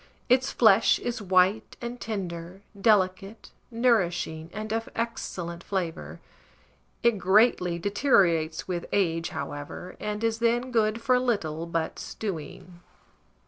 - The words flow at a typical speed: No, slow, 115 wpm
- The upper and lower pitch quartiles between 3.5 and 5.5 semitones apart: Yes, average, 4.9 semitones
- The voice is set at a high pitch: Yes, high, 195 Hz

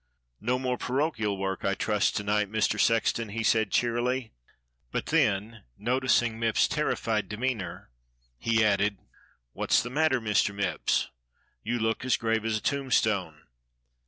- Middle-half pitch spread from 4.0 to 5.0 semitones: No, average, 2.9 semitones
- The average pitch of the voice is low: Yes, low, 110 Hz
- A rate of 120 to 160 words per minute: Yes, average, 155 wpm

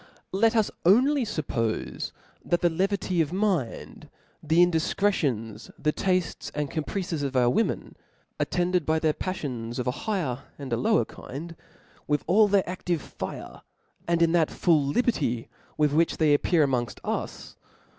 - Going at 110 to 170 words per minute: Yes, average, 155 wpm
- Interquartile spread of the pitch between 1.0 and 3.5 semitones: No, average, 4.9 semitones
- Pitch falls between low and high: Yes, medium, 165 Hz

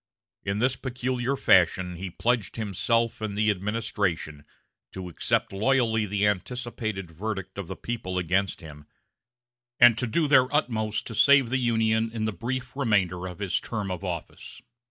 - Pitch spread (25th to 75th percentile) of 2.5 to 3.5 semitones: No, average, 4.2 semitones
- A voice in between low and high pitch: No, low, 110 Hz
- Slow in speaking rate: No, average, 155 wpm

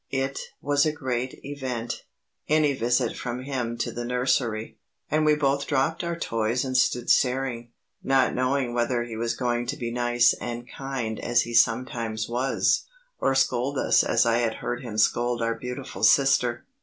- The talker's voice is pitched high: No, low, 125 Hz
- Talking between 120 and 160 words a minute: No, average, 170 wpm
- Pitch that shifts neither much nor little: No, narrow, 2.2 semitones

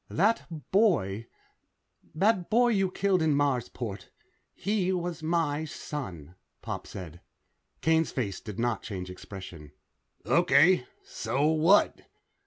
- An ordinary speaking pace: No, slow, 110 wpm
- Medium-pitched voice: Yes, medium, 150 Hz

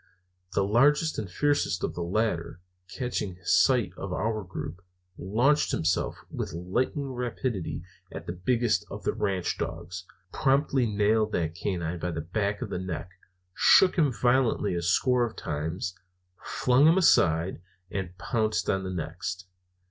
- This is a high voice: No, low, 100 Hz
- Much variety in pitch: Yes, wide, 5.8 semitones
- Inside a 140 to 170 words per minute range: Yes, average, 150 wpm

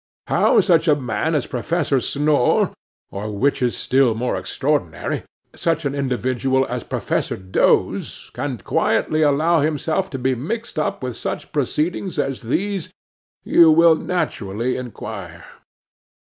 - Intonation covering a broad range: No, average, 4.3 semitones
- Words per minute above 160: No, slow, 135 wpm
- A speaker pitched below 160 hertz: Yes, medium, 140 Hz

